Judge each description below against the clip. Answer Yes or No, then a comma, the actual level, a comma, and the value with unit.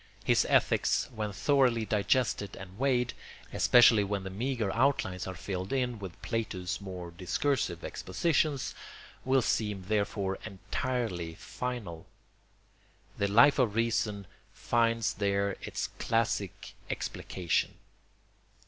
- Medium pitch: No, low, 105 Hz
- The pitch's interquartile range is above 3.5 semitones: Yes, average, 4.4 semitones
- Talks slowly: Yes, slow, 110 wpm